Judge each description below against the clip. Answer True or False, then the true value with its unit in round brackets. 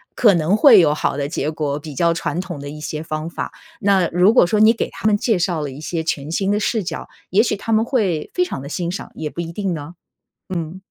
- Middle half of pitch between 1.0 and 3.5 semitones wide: False (4.8 semitones)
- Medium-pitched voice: True (170 Hz)